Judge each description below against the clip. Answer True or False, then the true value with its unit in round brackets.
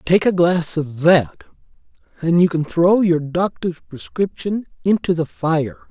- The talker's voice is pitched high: False (165 Hz)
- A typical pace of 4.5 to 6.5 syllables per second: False (4.2 syllables/s)